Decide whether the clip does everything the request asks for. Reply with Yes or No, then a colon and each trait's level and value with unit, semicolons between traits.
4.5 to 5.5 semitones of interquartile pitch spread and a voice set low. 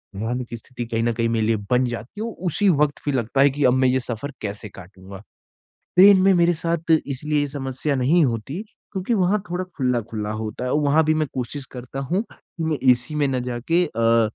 Yes: average, 5.2 semitones; low, 130 Hz